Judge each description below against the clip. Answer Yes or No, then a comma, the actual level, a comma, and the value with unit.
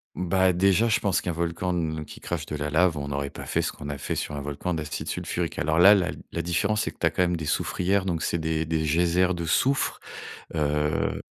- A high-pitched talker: No, very low, 85 Hz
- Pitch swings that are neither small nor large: Yes, average, 3.1 semitones